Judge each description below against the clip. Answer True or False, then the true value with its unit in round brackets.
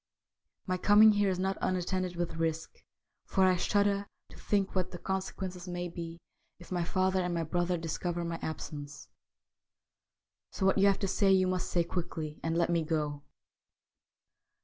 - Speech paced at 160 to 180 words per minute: True (170 wpm)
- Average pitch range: False (2.2 semitones)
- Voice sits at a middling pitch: True (180 Hz)